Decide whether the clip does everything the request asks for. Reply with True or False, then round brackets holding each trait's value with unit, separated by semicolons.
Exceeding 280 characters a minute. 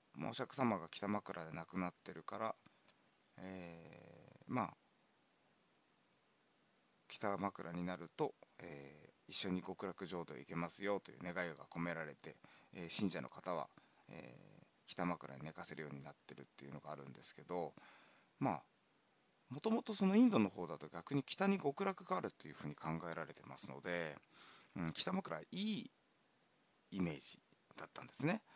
True (305 characters per minute)